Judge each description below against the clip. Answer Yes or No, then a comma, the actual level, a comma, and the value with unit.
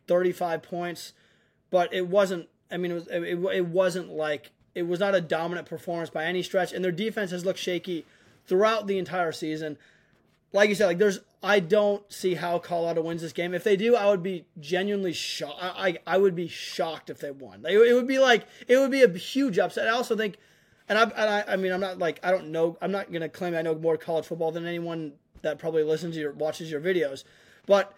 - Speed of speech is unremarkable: No, fast, 230 wpm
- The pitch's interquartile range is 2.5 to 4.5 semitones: Yes, average, 3.3 semitones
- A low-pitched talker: No, medium, 180 Hz